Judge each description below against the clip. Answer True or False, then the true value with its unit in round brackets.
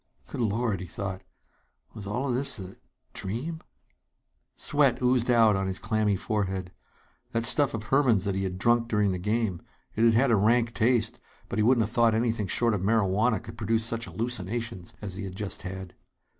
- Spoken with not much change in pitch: False (3.3 semitones)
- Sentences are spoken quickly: False (190 wpm)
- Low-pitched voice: True (110 Hz)